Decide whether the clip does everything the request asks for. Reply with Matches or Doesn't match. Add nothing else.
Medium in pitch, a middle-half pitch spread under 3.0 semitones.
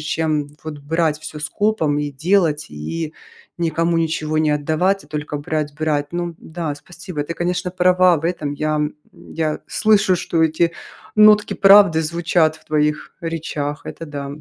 Matches